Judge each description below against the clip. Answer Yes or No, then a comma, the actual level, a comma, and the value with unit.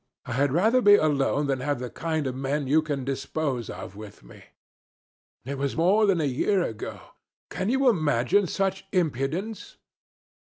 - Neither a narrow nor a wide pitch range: No, wide, 5.9 semitones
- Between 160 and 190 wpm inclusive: Yes, average, 165 wpm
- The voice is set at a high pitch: No, medium, 150 Hz